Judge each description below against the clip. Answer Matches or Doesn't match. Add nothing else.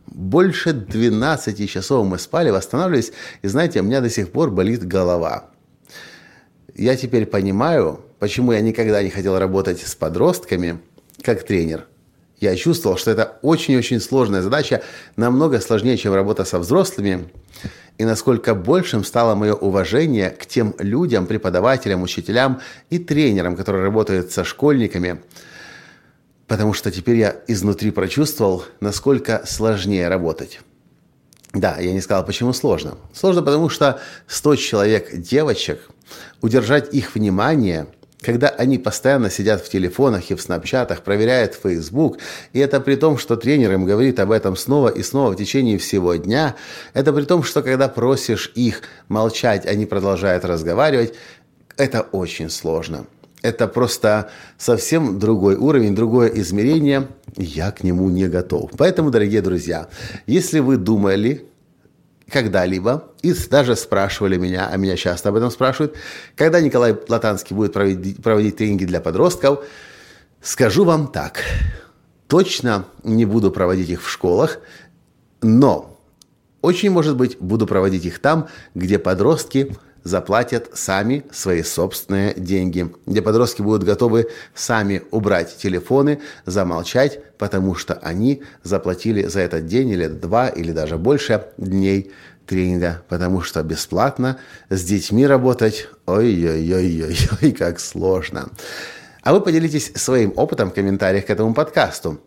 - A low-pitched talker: Matches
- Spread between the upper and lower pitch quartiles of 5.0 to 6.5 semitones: Matches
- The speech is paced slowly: Doesn't match